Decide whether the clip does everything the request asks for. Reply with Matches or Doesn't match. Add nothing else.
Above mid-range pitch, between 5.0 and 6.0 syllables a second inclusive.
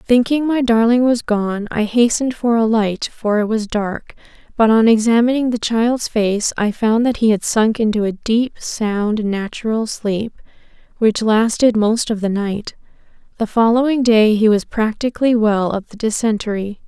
Doesn't match